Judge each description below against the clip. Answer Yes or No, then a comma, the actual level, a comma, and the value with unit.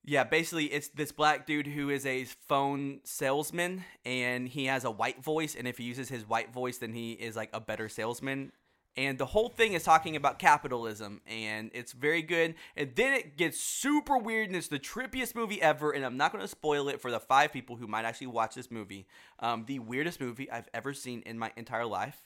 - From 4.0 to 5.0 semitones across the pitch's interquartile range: Yes, average, 4.6 semitones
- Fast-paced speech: Yes, fast, 225 wpm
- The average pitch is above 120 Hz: Yes, low, 135 Hz